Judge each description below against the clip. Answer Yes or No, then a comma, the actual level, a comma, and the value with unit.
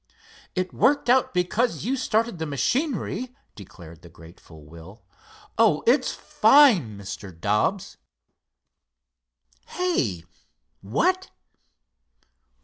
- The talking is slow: Yes, slow, 90 wpm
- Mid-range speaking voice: Yes, medium, 175 Hz